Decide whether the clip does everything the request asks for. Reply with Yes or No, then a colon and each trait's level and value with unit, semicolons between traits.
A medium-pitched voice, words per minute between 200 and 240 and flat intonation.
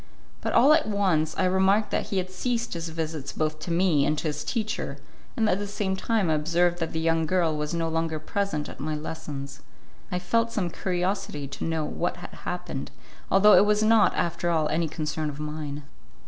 No: medium, 170 Hz; fast, 205 wpm; average, 4.0 semitones